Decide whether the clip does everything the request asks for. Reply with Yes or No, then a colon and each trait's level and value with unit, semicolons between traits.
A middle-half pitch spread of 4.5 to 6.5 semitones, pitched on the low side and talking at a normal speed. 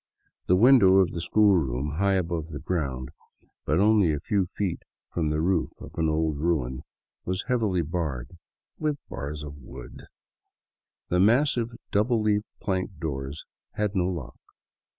Yes: average, 5.1 semitones; very low, 85 Hz; average, 155 wpm